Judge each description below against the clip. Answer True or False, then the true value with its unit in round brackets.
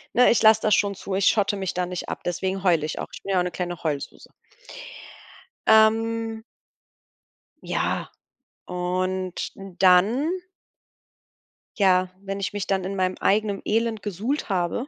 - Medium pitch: False (195 Hz)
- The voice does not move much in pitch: False (3.2 semitones)